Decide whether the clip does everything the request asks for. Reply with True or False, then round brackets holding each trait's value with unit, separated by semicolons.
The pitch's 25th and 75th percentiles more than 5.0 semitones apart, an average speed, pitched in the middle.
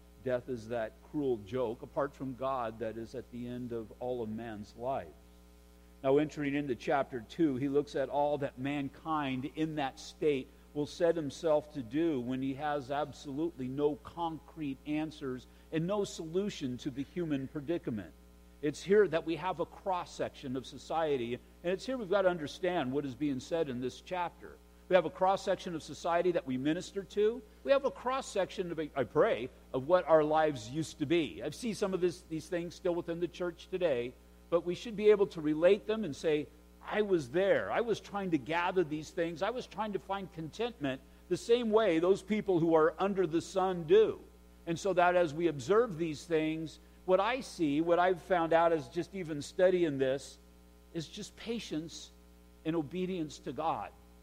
True (5.4 semitones; 195 wpm; 160 Hz)